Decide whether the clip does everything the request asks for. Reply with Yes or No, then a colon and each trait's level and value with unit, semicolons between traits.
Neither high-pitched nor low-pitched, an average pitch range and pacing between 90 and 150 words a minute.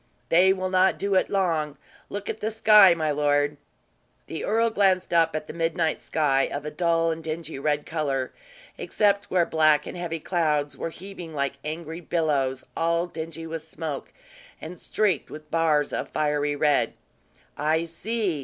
No: medium, 165 Hz; average, 3.1 semitones; average, 165 wpm